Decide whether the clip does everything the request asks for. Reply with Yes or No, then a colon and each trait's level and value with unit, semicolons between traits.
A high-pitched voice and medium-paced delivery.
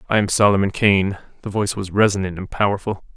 No: low, 100 Hz; average, 190 wpm